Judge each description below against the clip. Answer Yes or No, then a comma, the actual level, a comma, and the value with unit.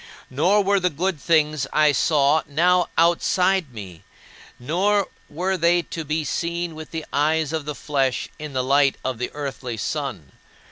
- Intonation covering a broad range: No, average, 3.8 semitones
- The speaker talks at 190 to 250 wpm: No, average, 155 wpm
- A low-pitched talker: No, medium, 155 Hz